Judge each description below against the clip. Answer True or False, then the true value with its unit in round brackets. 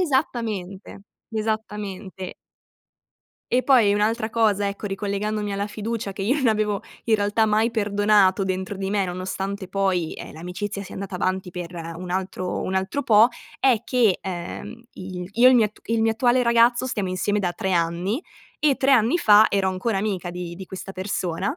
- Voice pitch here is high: True (205 Hz)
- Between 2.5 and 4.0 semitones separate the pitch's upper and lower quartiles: True (2.9 semitones)